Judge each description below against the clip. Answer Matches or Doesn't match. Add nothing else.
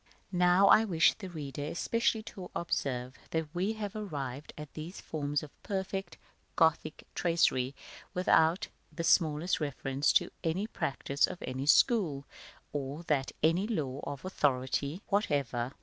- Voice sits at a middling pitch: Matches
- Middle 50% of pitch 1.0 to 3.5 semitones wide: Doesn't match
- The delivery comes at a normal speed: Matches